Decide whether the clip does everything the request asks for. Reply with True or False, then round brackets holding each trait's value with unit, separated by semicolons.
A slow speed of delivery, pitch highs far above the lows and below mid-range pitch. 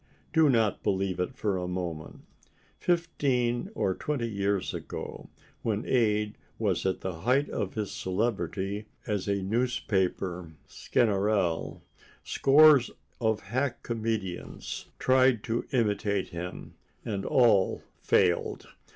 False (110 wpm; 4.2 semitones; 105 Hz)